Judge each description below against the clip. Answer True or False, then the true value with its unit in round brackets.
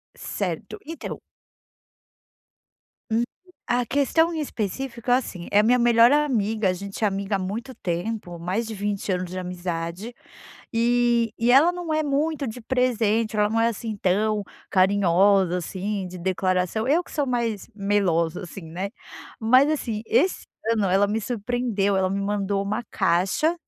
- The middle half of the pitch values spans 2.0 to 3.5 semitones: False (4.1 semitones)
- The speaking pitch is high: True (215 Hz)